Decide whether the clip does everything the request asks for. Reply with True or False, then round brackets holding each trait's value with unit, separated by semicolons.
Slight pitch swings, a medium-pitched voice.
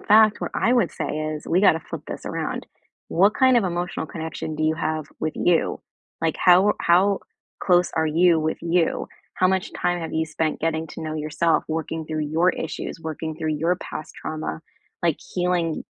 True (2.3 semitones; 165 Hz)